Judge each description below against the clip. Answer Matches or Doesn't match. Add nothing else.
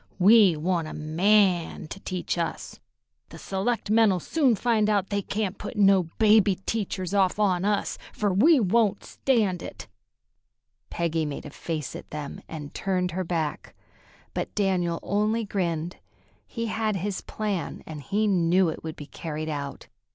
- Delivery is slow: Doesn't match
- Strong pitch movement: Doesn't match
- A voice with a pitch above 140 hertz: Matches